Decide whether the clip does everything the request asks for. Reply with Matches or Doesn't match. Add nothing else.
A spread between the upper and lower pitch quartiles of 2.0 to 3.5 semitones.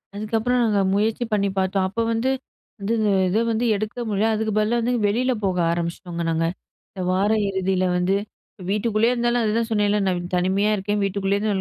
Matches